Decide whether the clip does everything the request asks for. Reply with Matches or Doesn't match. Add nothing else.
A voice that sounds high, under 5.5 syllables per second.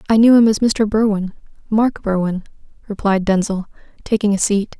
Matches